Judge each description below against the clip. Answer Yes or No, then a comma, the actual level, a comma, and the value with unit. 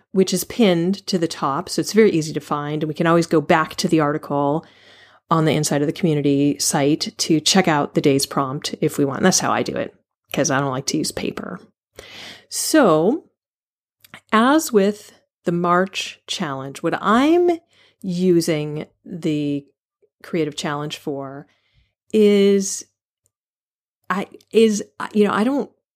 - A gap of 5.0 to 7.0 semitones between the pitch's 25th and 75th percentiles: Yes, wide, 5.4 semitones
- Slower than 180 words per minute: Yes, average, 160 wpm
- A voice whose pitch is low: No, medium, 170 Hz